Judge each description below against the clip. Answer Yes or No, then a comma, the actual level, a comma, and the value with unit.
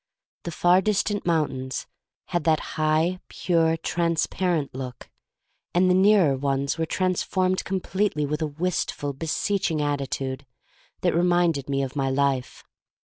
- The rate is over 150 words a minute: No, slow, 135 wpm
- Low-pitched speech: No, medium, 160 Hz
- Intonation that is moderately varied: Yes, average, 4.4 semitones